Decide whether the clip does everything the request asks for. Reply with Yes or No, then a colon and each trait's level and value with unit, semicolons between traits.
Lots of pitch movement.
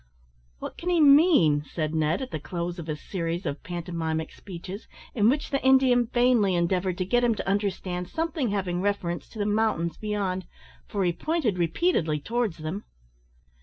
Yes: wide, 6.0 semitones